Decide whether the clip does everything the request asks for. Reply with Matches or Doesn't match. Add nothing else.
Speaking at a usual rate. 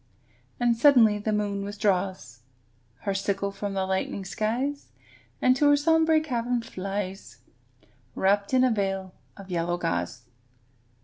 Doesn't match